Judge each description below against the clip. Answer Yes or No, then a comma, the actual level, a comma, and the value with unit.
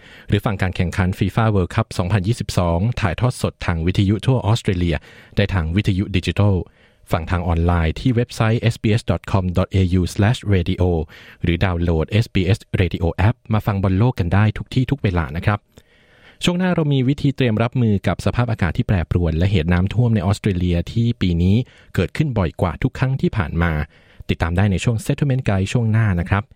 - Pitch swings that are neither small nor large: Yes, average, 4.1 semitones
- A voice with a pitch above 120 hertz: No, low, 100 Hz